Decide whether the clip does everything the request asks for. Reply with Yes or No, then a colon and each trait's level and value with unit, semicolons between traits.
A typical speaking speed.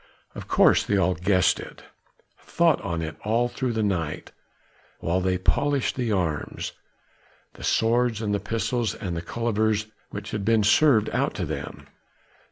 Yes: average, 165 wpm